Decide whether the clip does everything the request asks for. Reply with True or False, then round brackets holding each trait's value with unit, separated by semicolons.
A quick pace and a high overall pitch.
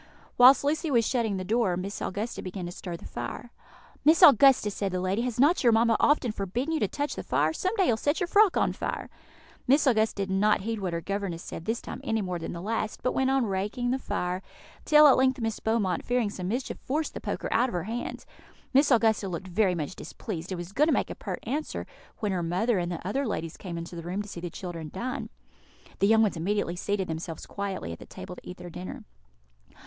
True (240 wpm; 205 Hz)